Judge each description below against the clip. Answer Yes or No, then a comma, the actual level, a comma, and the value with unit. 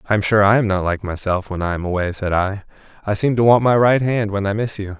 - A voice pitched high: No, low, 100 Hz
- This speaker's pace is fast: Yes, fast, 300 wpm